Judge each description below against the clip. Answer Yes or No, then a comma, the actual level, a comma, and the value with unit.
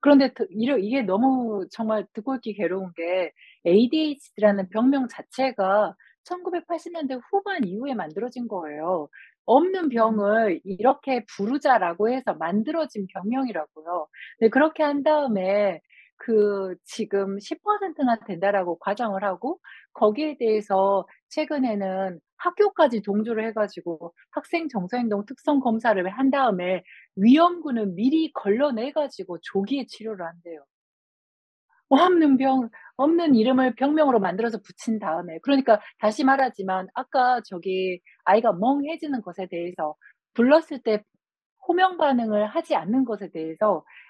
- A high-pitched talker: Yes, high, 225 Hz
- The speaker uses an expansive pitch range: Yes, wide, 5.9 semitones